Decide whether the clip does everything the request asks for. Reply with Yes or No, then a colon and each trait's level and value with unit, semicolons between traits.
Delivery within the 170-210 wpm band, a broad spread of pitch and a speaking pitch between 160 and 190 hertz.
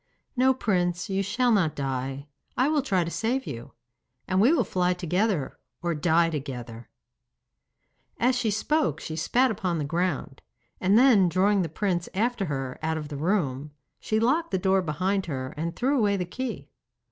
Yes: average, 175 wpm; wide, 6.1 semitones; medium, 185 Hz